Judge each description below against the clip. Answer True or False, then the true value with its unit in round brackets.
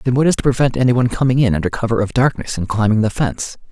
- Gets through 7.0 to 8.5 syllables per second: True (7.3 syllables/s)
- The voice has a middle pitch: False (120 Hz)